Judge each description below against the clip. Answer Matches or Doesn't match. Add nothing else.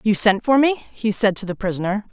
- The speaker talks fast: Matches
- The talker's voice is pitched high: Matches